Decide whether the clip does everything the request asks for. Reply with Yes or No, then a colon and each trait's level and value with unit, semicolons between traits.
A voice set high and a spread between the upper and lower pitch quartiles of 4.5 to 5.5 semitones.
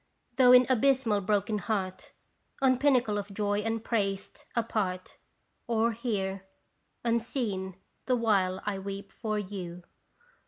No: high, 210 Hz; average, 3.1 semitones